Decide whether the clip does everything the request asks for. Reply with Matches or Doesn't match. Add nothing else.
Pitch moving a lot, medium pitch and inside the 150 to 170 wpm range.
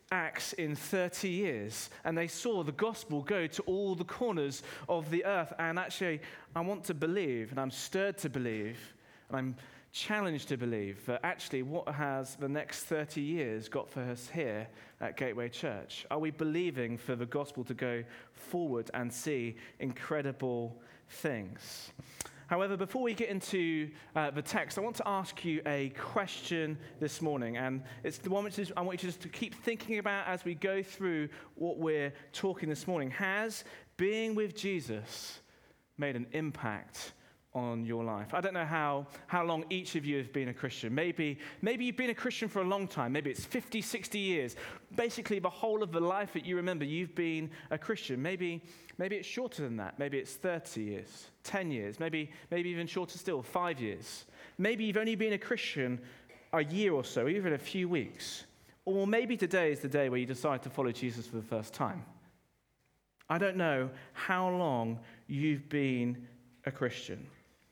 Doesn't match